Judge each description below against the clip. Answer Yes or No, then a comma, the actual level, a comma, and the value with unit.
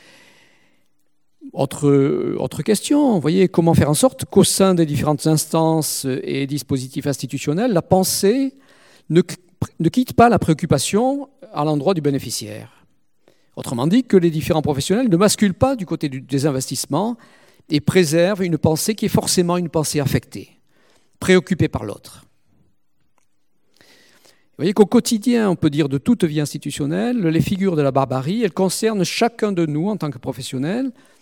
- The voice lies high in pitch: No, medium, 165 Hz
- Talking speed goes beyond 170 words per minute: No, average, 155 wpm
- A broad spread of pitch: Yes, wide, 5.7 semitones